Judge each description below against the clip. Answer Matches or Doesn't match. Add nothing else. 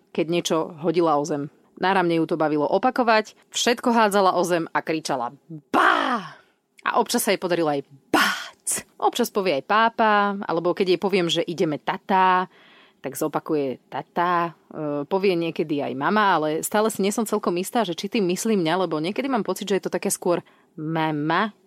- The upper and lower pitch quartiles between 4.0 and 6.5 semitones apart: Matches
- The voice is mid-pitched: Matches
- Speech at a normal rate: Doesn't match